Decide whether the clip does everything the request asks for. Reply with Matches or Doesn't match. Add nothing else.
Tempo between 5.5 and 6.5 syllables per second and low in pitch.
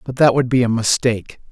Matches